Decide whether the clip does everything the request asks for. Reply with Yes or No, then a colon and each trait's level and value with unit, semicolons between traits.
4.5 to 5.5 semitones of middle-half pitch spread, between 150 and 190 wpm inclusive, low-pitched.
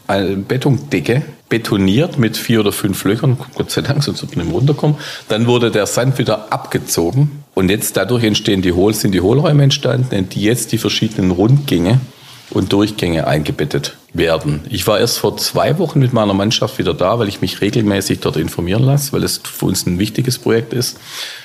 Yes: average, 4.8 semitones; average, 185 wpm; low, 110 Hz